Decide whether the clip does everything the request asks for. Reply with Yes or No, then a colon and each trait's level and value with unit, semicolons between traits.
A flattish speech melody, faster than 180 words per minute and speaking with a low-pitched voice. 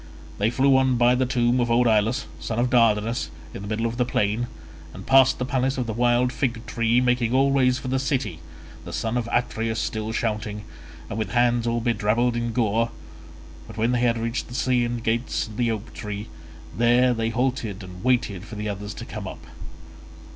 Yes: narrow, 1.9 semitones; average, 195 wpm; low, 120 Hz